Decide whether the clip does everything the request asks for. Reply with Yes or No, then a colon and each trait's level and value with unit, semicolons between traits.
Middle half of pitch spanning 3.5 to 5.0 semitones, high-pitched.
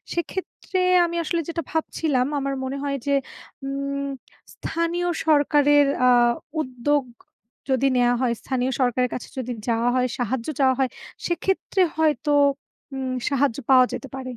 No: average, 3.1 semitones; very high, 275 Hz